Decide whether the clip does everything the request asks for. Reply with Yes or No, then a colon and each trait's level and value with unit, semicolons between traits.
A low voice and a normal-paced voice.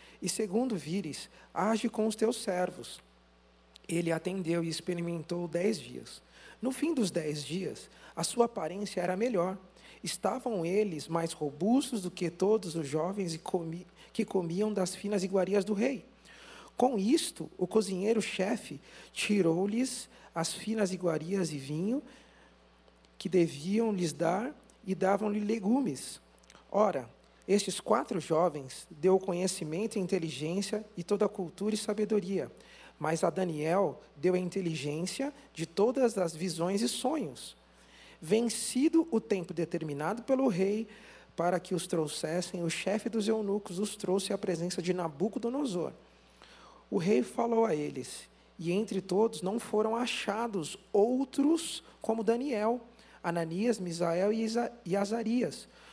No: high, 190 Hz; average, 130 wpm